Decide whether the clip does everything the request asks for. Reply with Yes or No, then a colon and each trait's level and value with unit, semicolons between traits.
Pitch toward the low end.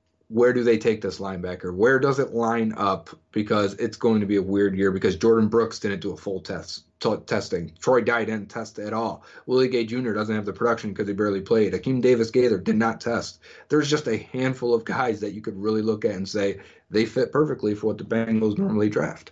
Yes: low, 110 Hz